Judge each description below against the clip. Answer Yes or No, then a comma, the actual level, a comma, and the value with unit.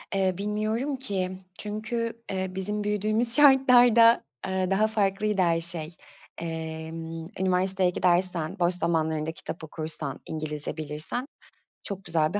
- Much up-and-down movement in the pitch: No, average, 4.6 semitones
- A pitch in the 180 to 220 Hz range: Yes, medium, 185 Hz